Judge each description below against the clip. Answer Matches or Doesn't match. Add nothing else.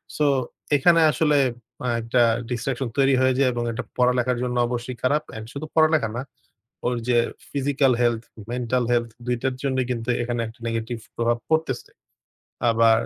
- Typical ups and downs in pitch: Doesn't match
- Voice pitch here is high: Doesn't match